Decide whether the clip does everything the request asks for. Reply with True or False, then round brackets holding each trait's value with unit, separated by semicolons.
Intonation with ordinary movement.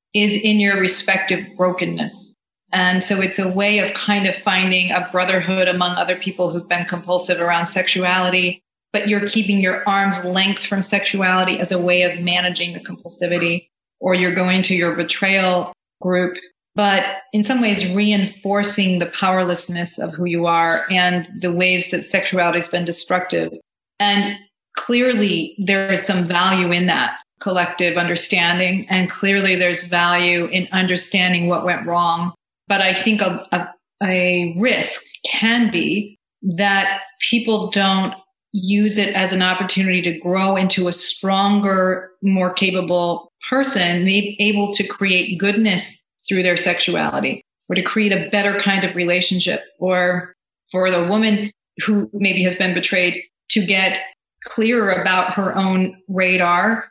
False (1.9 semitones)